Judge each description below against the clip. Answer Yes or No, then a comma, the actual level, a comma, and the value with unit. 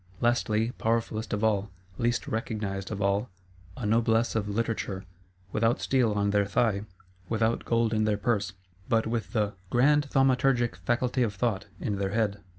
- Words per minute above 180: No, average, 155 wpm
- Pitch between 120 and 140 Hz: No, low, 110 Hz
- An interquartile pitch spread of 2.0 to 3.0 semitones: Yes, narrow, 2.5 semitones